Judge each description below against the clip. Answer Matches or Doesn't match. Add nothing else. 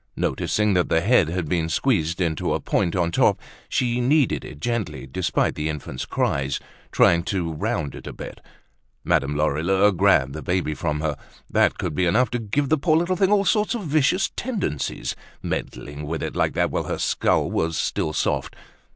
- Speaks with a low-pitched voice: Matches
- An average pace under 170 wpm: Doesn't match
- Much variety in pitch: Matches